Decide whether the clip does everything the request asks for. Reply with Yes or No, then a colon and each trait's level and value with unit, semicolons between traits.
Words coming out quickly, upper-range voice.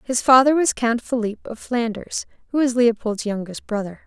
No: average, 175 wpm; high, 230 Hz